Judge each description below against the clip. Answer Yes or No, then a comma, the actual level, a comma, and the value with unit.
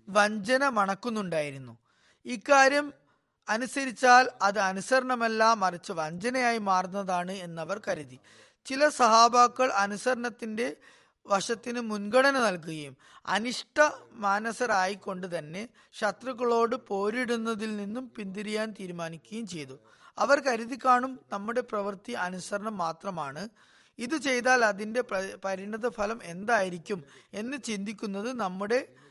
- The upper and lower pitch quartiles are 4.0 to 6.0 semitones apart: Yes, average, 4.3 semitones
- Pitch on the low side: No, high, 215 Hz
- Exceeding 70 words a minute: Yes, average, 90 wpm